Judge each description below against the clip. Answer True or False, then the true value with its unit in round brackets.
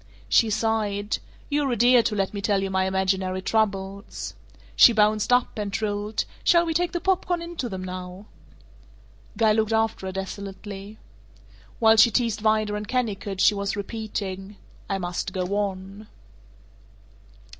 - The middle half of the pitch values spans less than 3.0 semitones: True (2.4 semitones)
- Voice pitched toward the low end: False (210 Hz)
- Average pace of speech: True (155 wpm)